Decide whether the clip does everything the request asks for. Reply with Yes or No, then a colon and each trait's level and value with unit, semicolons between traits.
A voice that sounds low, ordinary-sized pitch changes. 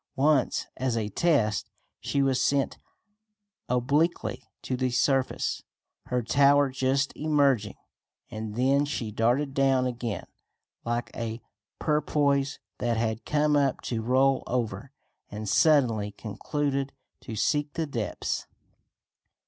Yes: low, 130 Hz; average, 3.5 semitones